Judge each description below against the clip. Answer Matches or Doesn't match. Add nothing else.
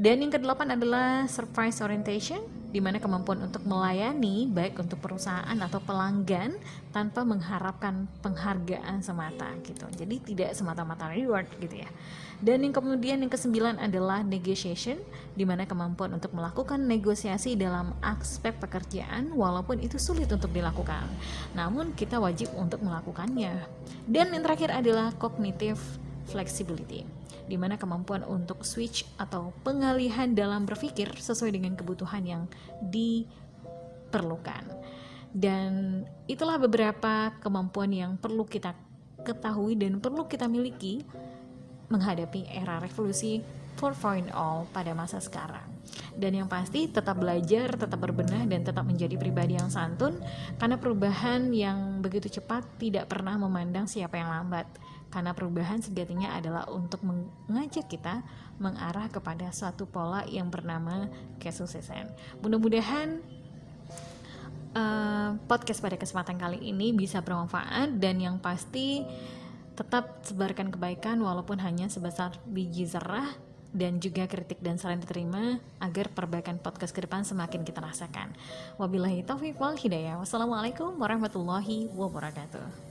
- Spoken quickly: Doesn't match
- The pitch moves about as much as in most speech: Matches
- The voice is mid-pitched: Doesn't match